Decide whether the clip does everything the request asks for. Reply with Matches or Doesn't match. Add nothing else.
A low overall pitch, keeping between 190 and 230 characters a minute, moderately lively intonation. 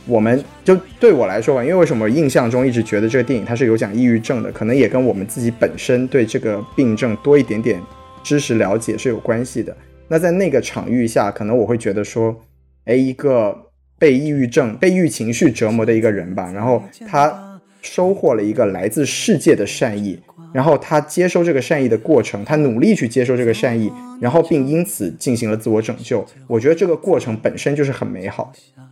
Doesn't match